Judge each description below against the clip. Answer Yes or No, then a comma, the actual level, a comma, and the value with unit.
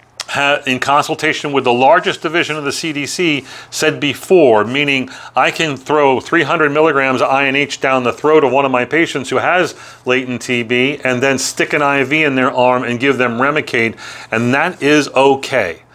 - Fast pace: No, average, 175 wpm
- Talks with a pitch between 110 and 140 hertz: Yes, low, 135 Hz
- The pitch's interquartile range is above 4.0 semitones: No, average, 2.8 semitones